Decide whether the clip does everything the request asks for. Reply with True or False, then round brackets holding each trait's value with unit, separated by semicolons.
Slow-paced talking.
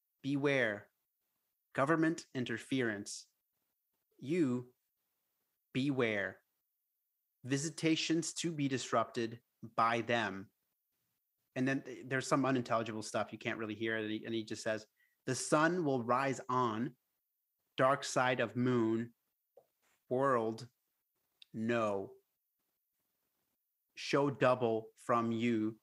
True (95 wpm)